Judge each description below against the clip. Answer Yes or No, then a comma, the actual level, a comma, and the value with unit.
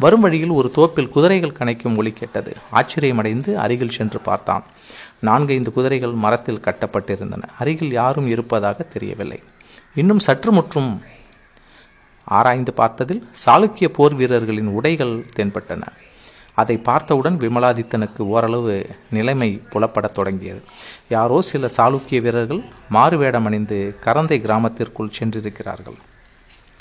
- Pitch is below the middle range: Yes, low, 120 Hz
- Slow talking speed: No, average, 105 wpm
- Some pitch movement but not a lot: Yes, average, 4.4 semitones